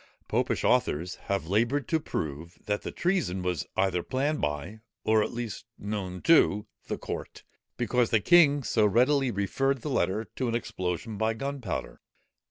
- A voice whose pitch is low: Yes, low, 110 Hz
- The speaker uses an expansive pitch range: Yes, wide, 6.3 semitones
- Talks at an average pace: Yes, average, 160 wpm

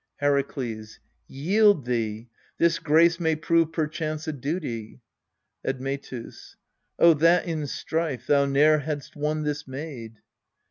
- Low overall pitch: No, medium, 150 Hz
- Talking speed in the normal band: No, slow, 120 wpm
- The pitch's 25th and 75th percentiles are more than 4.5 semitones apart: No, average, 3.3 semitones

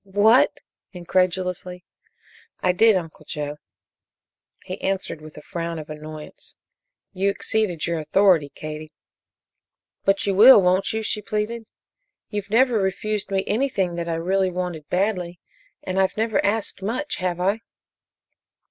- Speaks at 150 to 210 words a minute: No, slow, 135 wpm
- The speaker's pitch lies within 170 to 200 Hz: Yes, medium, 185 Hz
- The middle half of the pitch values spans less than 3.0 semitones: No, average, 3.7 semitones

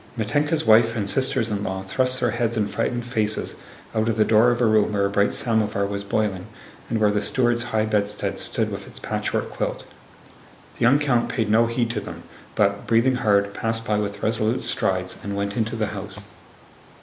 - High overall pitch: No, low, 110 Hz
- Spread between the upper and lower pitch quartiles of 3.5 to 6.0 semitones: No, narrow, 2.5 semitones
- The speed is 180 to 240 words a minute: Yes, average, 200 wpm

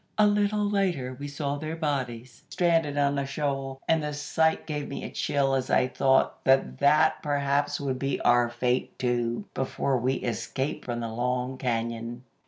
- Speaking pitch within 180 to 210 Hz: No, low, 135 Hz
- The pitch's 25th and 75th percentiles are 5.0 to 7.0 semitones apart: No, average, 2.8 semitones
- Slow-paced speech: No, average, 175 wpm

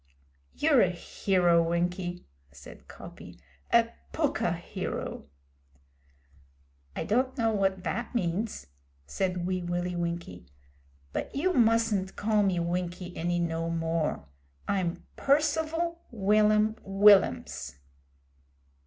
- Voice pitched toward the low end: No, high, 190 Hz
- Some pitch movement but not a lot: Yes, average, 4.3 semitones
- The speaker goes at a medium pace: No, slow, 100 wpm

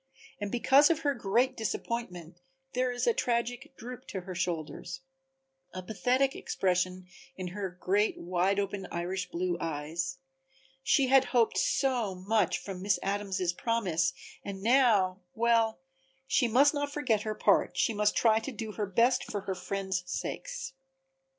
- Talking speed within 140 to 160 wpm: Yes, average, 150 wpm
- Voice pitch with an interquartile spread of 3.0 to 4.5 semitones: No, average, 4.9 semitones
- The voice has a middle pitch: No, high, 210 Hz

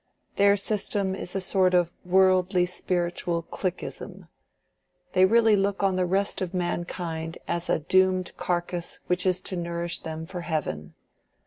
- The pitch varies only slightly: Yes, narrow, 1.6 semitones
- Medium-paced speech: Yes, average, 145 wpm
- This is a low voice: No, medium, 180 Hz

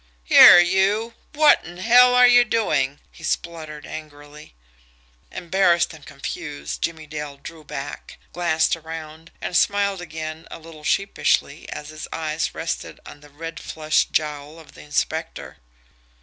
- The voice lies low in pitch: No, medium, 160 Hz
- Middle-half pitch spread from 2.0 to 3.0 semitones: Yes, narrow, 2.6 semitones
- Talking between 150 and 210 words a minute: No, average, 140 wpm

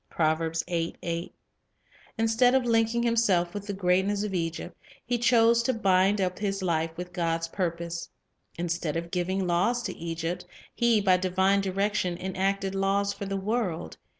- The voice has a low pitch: No, high, 190 Hz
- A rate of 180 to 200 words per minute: No, average, 150 wpm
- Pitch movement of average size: Yes, average, 3.3 semitones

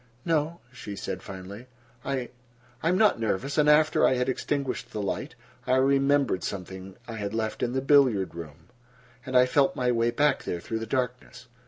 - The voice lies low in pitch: Yes, low, 125 Hz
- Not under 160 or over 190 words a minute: Yes, average, 180 wpm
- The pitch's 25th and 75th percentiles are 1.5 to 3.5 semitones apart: No, average, 4.1 semitones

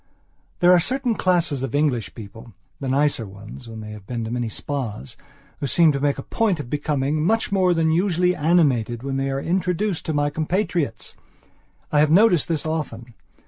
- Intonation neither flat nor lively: No, wide, 6.0 semitones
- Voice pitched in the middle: Yes, medium, 145 Hz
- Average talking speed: Yes, average, 185 wpm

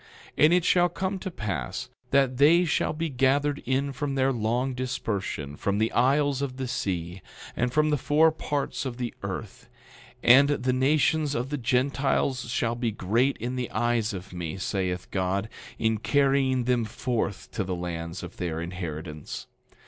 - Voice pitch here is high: No, low, 125 Hz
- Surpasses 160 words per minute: Yes, average, 170 wpm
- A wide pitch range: Yes, wide, 5.8 semitones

